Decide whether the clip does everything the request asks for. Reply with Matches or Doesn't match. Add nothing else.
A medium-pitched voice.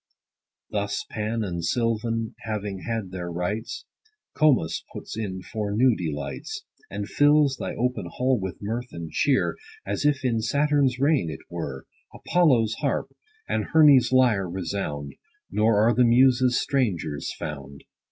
Doesn't match